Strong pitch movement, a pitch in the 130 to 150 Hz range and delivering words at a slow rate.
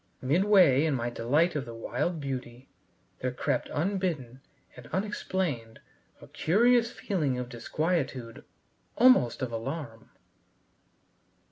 Yes: wide, 6.8 semitones; medium, 140 Hz; slow, 110 wpm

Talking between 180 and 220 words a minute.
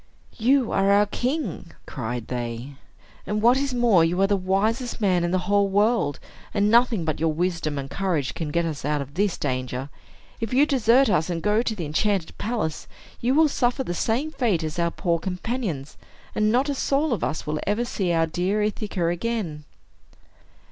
Yes: average, 190 wpm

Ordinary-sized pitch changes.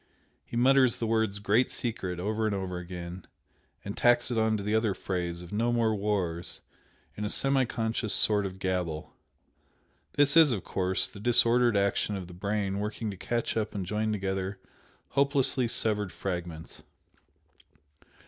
Yes: average, 3.6 semitones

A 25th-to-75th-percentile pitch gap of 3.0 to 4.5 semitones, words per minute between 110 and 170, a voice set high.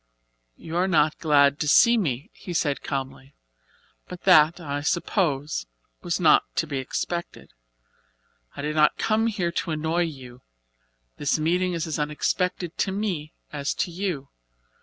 No: average, 3.7 semitones; average, 150 wpm; medium, 155 Hz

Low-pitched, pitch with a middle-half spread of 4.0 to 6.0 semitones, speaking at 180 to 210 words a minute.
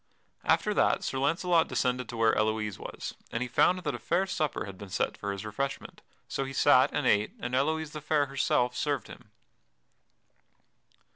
Yes: low, 130 Hz; wide, 5.4 semitones; average, 185 wpm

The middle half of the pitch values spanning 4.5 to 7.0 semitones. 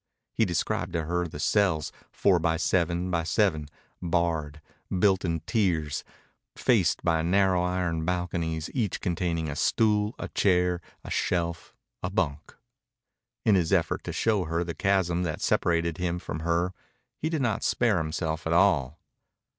No: narrow, 2.4 semitones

